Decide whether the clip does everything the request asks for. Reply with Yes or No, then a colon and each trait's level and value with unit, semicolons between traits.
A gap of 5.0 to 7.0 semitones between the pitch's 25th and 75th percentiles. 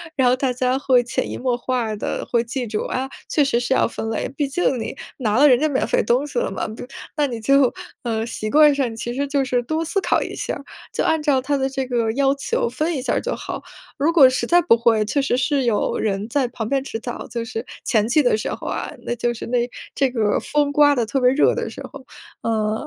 No: average, 3.2 semitones